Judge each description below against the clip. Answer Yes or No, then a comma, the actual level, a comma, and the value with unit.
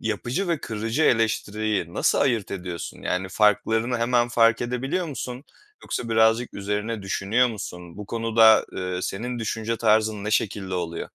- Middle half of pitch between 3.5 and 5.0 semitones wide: No, average, 2.8 semitones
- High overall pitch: No, low, 110 Hz